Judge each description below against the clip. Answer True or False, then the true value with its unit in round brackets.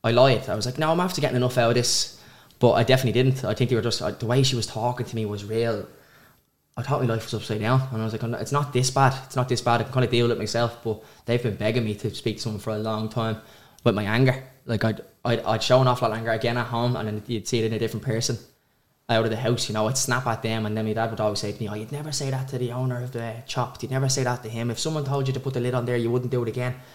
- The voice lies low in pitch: True (120 Hz)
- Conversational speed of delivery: False (320 wpm)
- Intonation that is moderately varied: False (2.2 semitones)